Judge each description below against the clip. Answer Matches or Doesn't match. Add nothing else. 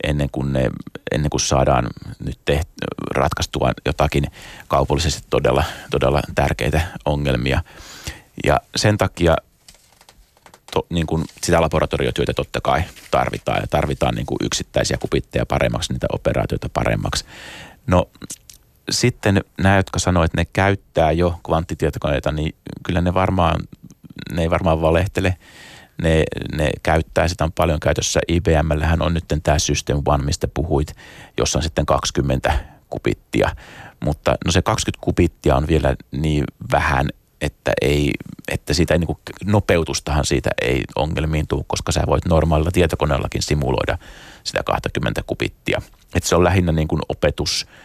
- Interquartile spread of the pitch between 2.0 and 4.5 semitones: Matches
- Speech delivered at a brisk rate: Doesn't match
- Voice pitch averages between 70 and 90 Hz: Matches